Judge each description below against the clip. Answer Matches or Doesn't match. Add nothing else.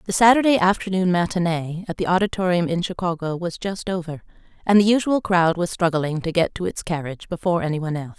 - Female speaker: Matches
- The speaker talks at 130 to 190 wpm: Doesn't match